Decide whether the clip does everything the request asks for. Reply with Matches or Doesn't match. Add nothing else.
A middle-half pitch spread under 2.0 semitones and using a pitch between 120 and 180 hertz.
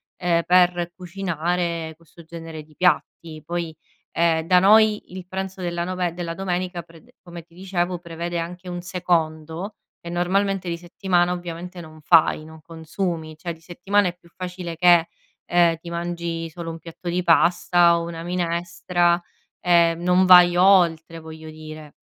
Matches